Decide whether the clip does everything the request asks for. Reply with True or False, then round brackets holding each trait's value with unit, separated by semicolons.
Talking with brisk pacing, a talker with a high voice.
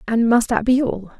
True (250 wpm; 230 Hz)